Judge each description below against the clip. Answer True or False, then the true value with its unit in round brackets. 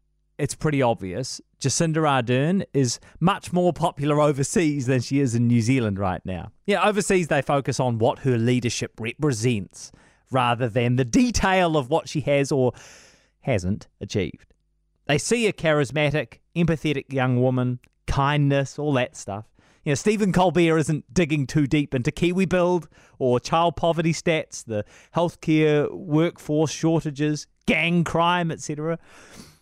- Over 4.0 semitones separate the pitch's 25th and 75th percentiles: True (4.5 semitones)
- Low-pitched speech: False (145 Hz)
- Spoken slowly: False (145 wpm)